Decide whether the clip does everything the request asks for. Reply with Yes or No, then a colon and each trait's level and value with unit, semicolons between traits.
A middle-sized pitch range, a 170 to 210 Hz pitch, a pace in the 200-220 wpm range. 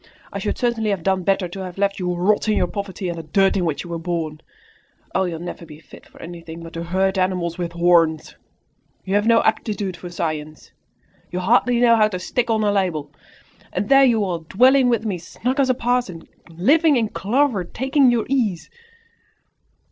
Yes: average, 4.9 semitones; high, 190 Hz; fast, 205 wpm